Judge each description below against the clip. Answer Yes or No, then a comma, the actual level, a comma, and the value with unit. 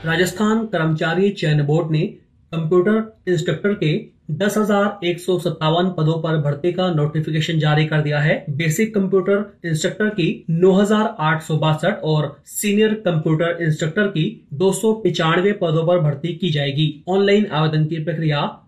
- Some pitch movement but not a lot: Yes, average, 3.5 semitones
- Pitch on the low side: No, medium, 170 Hz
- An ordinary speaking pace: Yes, average, 155 wpm